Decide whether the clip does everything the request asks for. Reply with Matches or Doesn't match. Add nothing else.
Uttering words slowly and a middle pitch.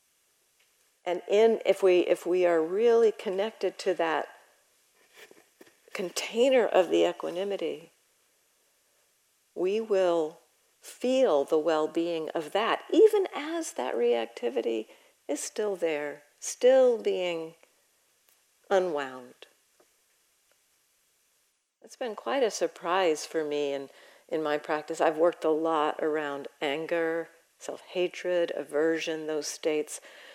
Matches